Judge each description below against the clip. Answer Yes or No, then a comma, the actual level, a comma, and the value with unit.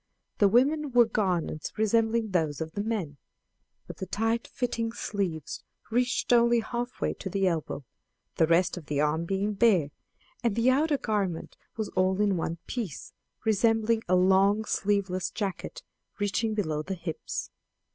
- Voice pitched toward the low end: No, high, 205 Hz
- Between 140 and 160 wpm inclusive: Yes, average, 150 wpm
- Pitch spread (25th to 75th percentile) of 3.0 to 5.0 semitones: Yes, average, 4.3 semitones